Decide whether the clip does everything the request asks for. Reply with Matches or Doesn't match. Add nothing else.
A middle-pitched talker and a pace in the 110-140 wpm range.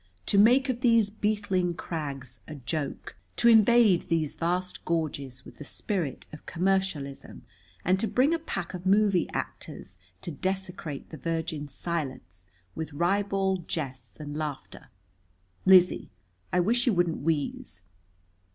Matches